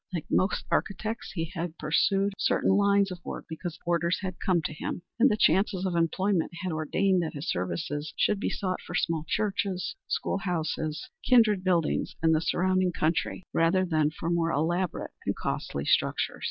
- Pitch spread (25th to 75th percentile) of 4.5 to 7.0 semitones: No, average, 3.2 semitones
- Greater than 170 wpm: Yes, average, 180 wpm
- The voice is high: No, medium, 175 Hz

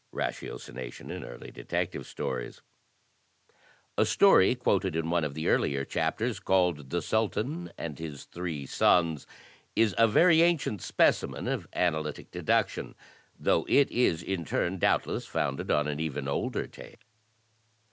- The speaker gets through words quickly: No, slow, 135 wpm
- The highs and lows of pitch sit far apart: Yes, wide, 6.2 semitones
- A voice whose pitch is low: Yes, very low, 85 Hz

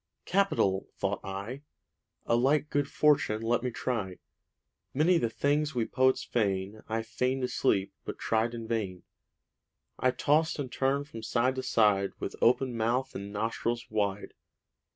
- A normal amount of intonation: Yes, average, 3.8 semitones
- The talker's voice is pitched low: Yes, low, 120 Hz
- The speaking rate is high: No, average, 150 wpm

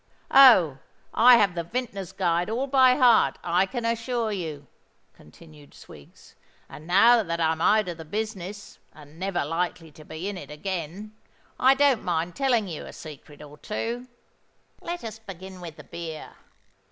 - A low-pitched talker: No, medium, 185 Hz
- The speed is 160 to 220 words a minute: Yes, average, 165 wpm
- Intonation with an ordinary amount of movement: No, wide, 5.9 semitones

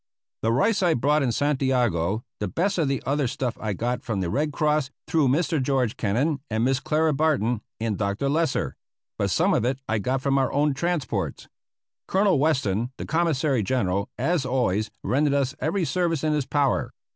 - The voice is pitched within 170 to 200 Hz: No, low, 135 Hz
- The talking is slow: No, average, 185 wpm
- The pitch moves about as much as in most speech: Yes, average, 4.6 semitones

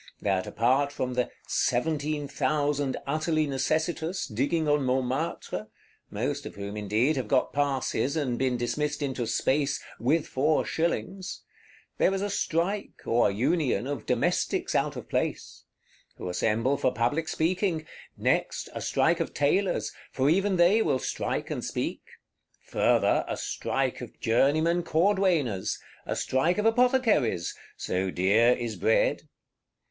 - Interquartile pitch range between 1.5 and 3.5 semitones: No, average, 5.2 semitones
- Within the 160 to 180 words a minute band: No, slow, 135 wpm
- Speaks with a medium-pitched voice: Yes, medium, 145 Hz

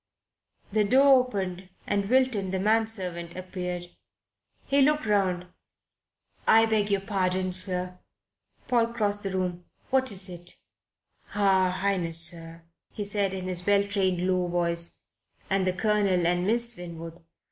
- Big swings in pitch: No, average, 2.7 semitones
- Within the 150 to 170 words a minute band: No, average, 140 wpm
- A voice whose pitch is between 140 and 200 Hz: Yes, high, 190 Hz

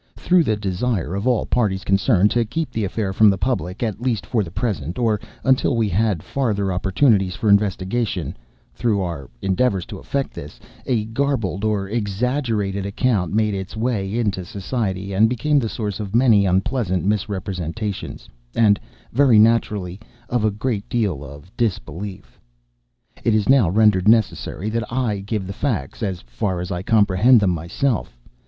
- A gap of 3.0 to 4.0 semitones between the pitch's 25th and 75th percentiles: Yes, average, 3.6 semitones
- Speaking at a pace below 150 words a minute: No, average, 155 wpm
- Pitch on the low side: Yes, low, 105 Hz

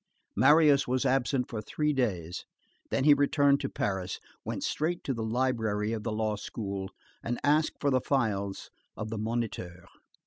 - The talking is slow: No, average, 165 wpm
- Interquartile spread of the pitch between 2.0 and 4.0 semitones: No, average, 4.8 semitones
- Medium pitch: No, low, 120 Hz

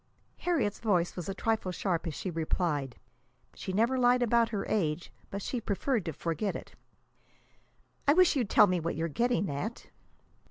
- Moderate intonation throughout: No, wide, 5.8 semitones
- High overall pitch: Yes, high, 200 Hz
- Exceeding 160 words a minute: Yes, average, 170 wpm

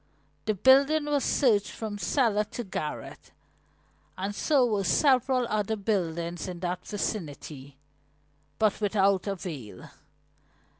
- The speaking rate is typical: No, slow, 110 wpm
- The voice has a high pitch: Yes, high, 205 Hz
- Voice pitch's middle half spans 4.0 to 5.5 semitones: Yes, average, 5.1 semitones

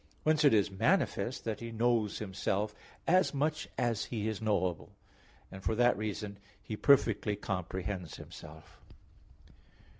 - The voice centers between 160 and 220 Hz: No, low, 110 Hz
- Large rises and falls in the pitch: No, average, 3.7 semitones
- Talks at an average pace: No, slow, 130 wpm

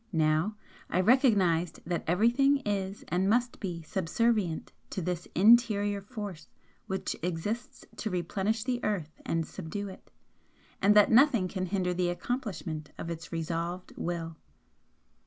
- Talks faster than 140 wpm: No, slow, 135 wpm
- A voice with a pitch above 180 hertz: Yes, high, 190 Hz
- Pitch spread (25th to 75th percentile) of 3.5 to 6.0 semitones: Yes, average, 4.3 semitones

